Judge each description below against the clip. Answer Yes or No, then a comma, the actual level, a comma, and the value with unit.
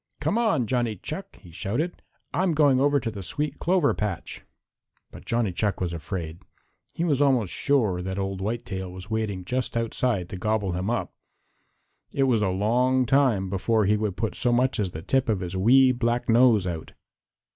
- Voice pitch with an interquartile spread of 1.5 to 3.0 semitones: No, average, 5.3 semitones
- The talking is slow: No, average, 185 wpm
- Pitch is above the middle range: No, low, 110 Hz